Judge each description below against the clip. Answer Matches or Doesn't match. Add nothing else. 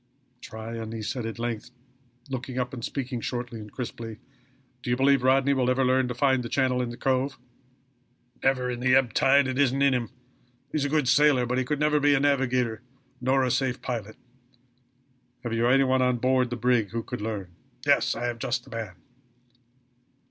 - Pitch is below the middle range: Matches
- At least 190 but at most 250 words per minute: Matches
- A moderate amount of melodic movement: Doesn't match